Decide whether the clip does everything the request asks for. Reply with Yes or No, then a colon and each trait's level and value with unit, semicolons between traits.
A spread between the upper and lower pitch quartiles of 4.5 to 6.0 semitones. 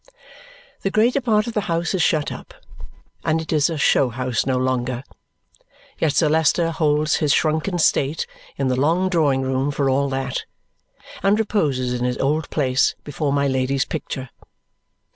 No: average, 3.9 semitones